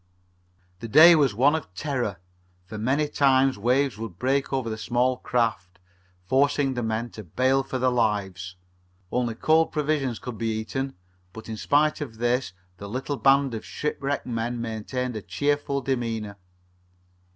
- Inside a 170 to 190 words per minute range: No, average, 155 wpm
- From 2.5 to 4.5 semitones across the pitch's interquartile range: Yes, average, 3.7 semitones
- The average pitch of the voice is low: Yes, low, 125 Hz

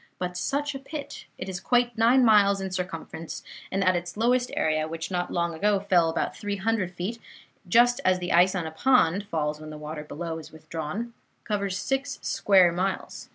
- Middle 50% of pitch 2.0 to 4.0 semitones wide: No, average, 5.2 semitones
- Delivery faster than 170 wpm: Yes, average, 195 wpm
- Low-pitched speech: No, medium, 185 Hz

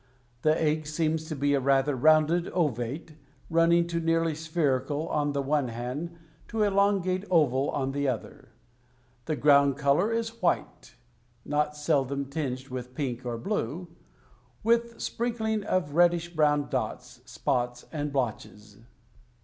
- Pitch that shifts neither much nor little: Yes, average, 4.1 semitones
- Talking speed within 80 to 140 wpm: Yes, slow, 135 wpm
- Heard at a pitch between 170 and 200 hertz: No, medium, 150 Hz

